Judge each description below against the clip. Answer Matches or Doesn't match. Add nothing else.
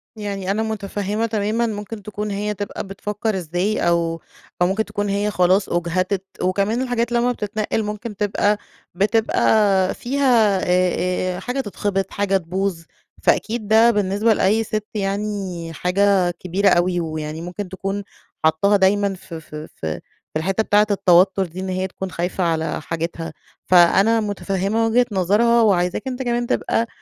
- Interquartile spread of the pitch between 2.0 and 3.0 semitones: Matches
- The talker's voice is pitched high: Matches